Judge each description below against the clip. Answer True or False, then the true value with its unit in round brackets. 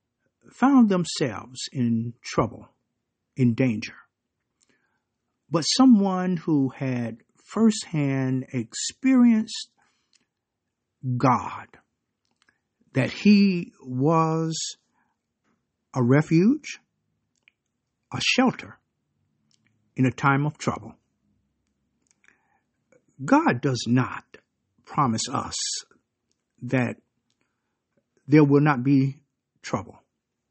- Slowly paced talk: True (70 wpm)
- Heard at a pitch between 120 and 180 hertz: True (135 Hz)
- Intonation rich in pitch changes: True (6.1 semitones)